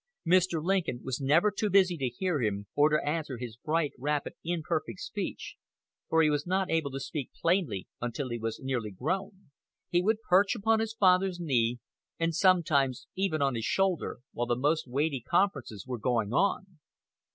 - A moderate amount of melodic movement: No, wide, 6.5 semitones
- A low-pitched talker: No, medium, 155 Hz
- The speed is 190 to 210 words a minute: No, average, 175 wpm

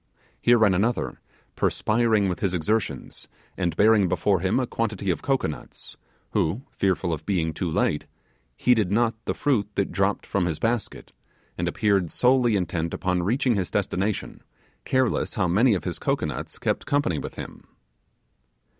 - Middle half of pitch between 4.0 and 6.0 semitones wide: Yes, average, 4.3 semitones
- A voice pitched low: Yes, low, 100 Hz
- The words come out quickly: No, average, 155 wpm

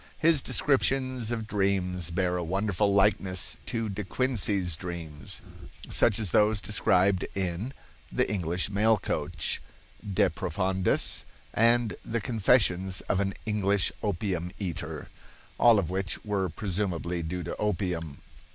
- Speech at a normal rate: No, slow, 125 wpm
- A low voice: Yes, very low, 95 Hz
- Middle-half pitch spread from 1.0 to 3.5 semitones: Yes, average, 3.1 semitones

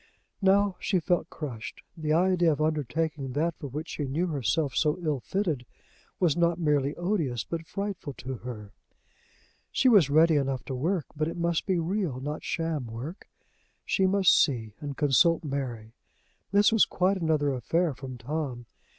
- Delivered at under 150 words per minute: No, average, 165 wpm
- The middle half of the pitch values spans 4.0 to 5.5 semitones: Yes, average, 4.4 semitones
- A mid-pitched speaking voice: Yes, medium, 155 Hz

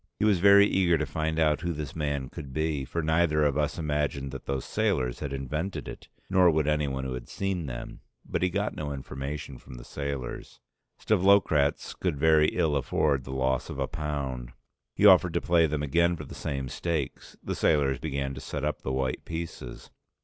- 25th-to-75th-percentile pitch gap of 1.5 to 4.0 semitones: Yes, average, 3.5 semitones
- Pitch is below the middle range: Yes, very low, 75 Hz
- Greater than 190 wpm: Yes, average, 200 wpm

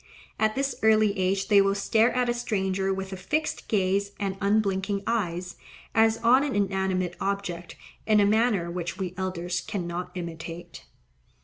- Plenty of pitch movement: No, average, 2.9 semitones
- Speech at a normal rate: Yes, average, 165 wpm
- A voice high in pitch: Yes, high, 195 Hz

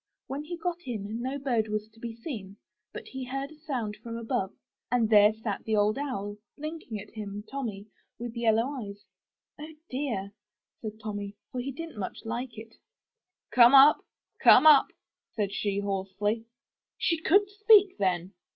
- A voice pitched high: Yes, high, 230 Hz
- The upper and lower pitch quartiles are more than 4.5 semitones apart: Yes, average, 5.0 semitones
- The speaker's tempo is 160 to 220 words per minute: Yes, average, 170 wpm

